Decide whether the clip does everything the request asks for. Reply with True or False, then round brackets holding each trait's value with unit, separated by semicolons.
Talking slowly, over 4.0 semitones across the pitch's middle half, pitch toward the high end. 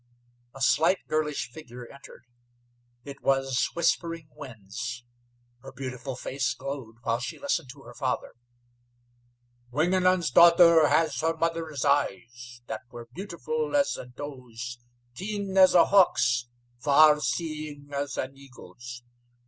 False (125 wpm; 5.1 semitones; 140 Hz)